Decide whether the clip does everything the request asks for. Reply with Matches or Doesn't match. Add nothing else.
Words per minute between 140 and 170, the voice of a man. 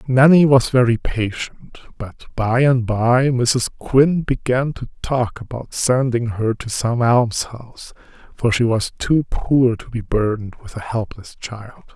Matches